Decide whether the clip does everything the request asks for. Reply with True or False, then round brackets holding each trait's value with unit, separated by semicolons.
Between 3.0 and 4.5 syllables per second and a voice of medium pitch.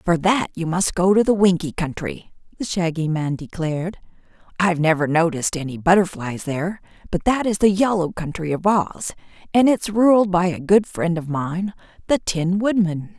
False (5.0 syllables/s; 180 Hz)